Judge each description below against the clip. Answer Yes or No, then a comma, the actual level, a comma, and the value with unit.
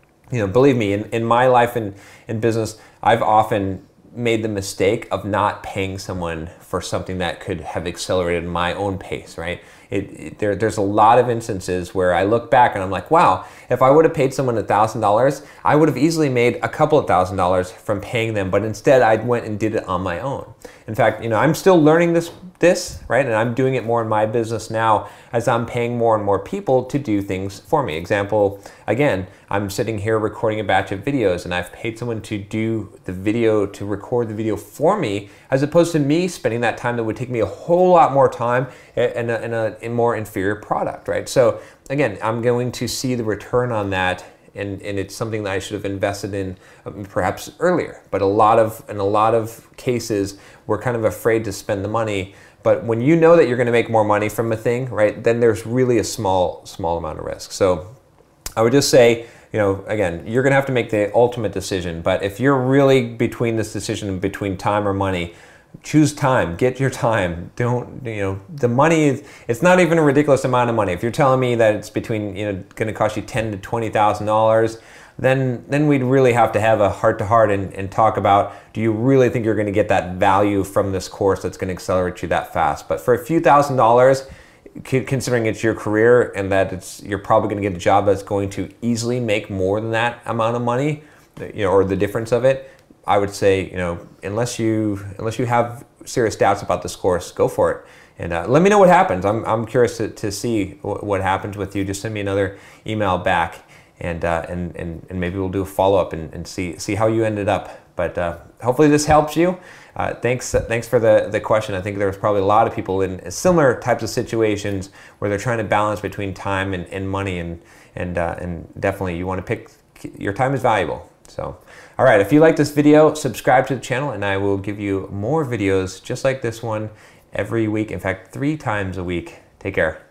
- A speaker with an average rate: No, fast, 230 wpm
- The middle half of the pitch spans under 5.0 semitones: Yes, average, 3.9 semitones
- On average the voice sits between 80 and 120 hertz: Yes, low, 110 Hz